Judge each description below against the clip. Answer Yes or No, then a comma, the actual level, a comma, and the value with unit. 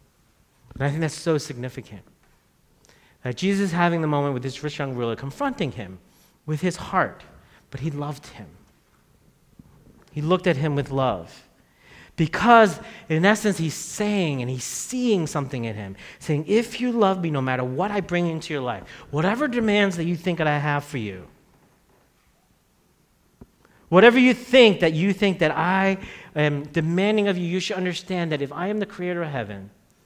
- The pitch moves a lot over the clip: Yes, wide, 6.0 semitones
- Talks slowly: No, average, 180 wpm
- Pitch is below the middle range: No, medium, 160 Hz